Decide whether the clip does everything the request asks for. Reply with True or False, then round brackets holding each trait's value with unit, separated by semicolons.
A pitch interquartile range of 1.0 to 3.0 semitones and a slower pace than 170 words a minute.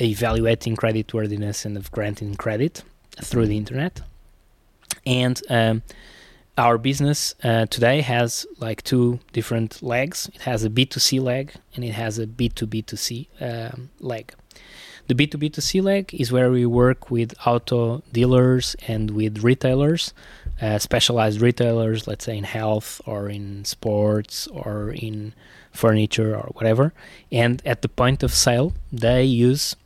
True (2.6 semitones; 135 wpm)